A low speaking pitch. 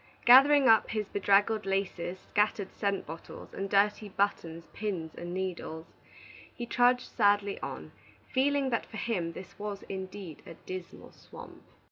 No: high, 200 Hz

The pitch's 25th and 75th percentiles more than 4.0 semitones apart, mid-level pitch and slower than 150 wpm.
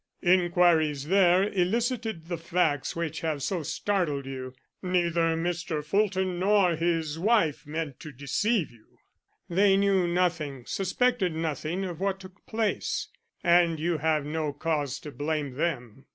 No: average, 3.7 semitones; medium, 170 Hz; average, 140 wpm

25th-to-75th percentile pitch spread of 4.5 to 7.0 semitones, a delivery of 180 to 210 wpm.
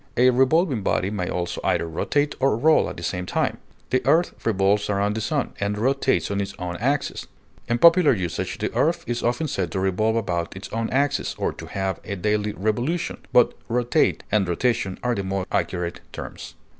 Yes: average, 5.1 semitones; average, 195 wpm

